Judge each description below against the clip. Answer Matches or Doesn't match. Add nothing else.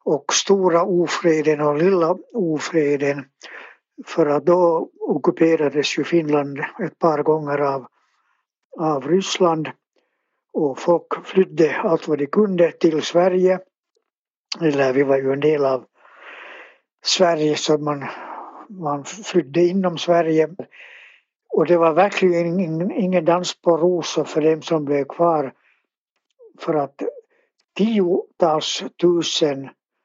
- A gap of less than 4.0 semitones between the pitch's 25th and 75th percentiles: Matches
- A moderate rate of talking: Doesn't match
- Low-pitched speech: Doesn't match